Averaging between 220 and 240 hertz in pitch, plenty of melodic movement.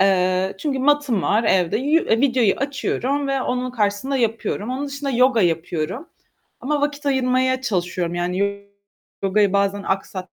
Yes: high, 235 Hz; wide, 5.8 semitones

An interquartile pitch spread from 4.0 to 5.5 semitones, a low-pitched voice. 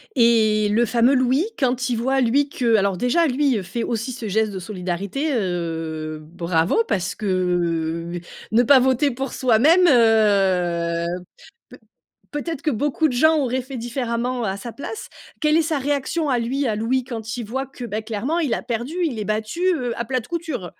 No: average, 4.8 semitones; high, 235 Hz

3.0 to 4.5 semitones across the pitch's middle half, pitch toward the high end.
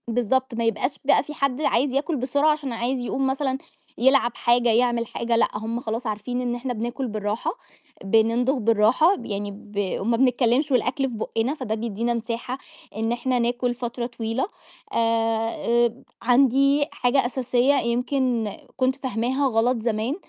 No: narrow, 2.5 semitones; high, 240 Hz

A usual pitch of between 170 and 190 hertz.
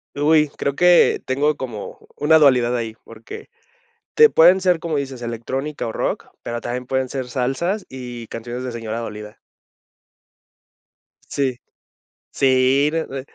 No: low, 130 Hz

